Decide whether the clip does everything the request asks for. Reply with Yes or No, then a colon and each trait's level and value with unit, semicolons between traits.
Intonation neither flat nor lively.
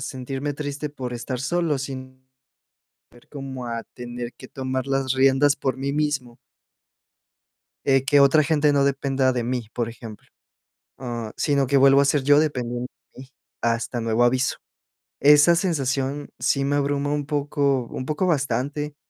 No: narrow, 2.2 semitones